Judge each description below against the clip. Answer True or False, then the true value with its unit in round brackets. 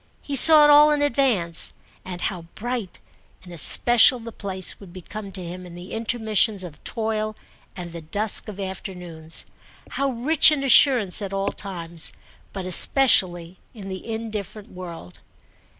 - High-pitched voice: True (200 Hz)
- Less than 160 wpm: True (150 wpm)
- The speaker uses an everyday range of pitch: True (4.5 semitones)